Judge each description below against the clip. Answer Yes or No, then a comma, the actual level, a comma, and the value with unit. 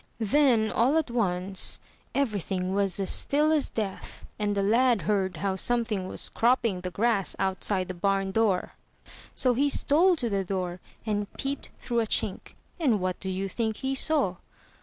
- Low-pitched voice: No, high, 210 Hz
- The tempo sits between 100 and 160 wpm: No, average, 170 wpm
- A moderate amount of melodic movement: Yes, average, 4.4 semitones